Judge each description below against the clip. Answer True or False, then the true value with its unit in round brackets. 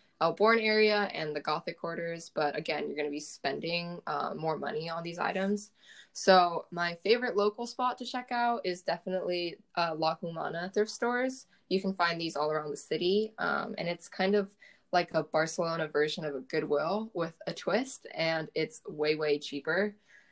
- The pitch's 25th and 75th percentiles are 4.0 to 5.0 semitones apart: True (4.6 semitones)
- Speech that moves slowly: False (185 wpm)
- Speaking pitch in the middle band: True (175 Hz)